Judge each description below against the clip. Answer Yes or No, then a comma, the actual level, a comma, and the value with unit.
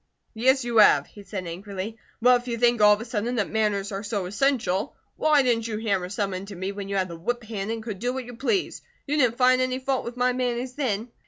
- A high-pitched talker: Yes, high, 225 Hz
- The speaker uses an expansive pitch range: No, average, 3.9 semitones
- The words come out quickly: Yes, fast, 250 wpm